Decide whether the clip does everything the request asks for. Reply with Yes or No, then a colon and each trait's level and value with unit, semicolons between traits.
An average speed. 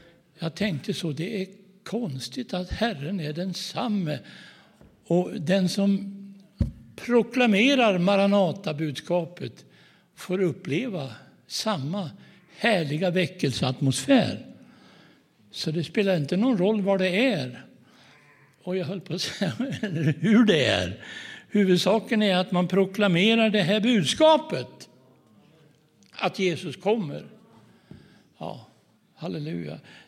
No: slow, 100 wpm